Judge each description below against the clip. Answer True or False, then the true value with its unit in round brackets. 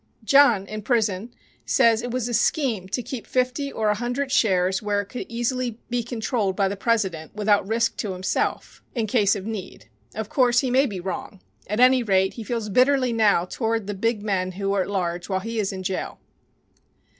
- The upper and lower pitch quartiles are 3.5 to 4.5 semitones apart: True (3.8 semitones)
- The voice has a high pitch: True (220 Hz)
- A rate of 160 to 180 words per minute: False (200 wpm)